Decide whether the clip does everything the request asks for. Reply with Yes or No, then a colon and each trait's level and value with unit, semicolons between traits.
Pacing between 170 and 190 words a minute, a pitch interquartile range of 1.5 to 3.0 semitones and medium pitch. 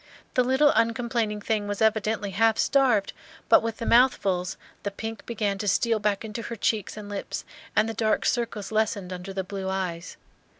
No: average, 180 wpm; narrow, 2.4 semitones; high, 215 Hz